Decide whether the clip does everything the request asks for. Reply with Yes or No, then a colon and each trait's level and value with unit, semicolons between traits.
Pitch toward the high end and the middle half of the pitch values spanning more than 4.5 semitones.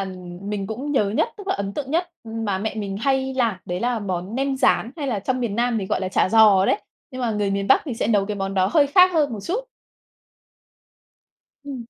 Yes: high, 225 Hz; average, 5.2 semitones